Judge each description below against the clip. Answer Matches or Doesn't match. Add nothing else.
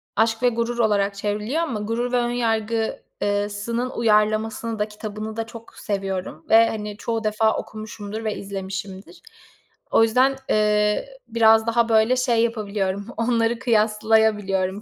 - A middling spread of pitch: Doesn't match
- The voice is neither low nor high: Doesn't match